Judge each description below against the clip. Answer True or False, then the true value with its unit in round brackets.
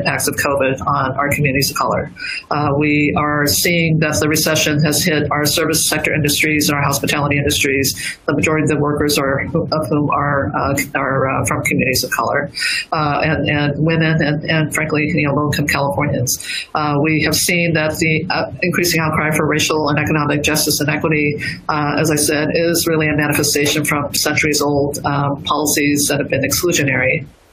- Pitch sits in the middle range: True (150 Hz)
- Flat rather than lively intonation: True (1.2 semitones)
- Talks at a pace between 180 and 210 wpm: True (185 wpm)